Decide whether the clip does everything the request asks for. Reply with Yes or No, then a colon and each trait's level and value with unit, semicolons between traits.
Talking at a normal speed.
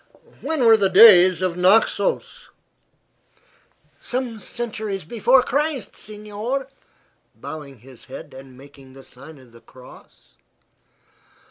No: slow, 110 wpm